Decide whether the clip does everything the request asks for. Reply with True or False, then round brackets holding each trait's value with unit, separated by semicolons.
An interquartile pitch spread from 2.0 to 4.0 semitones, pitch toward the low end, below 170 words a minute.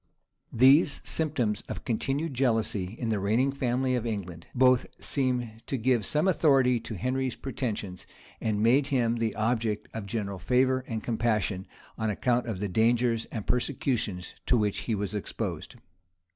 True (3.3 semitones; 115 Hz; 155 wpm)